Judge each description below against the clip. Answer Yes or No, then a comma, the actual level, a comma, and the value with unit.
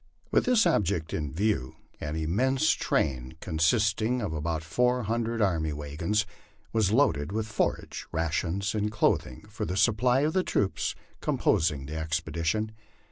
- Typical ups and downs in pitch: No, wide, 5.8 semitones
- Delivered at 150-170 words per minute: No, average, 140 wpm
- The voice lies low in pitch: Yes, very low, 95 Hz